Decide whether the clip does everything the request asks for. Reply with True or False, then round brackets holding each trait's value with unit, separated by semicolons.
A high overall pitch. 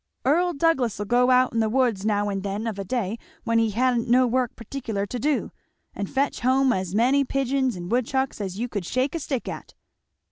True (240 Hz)